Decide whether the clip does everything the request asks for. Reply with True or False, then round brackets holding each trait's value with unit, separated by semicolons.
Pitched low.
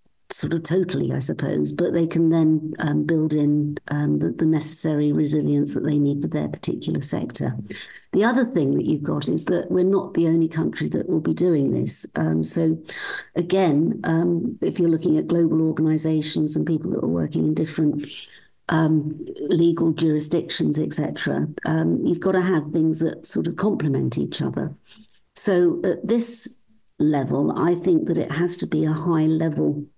False (160 Hz)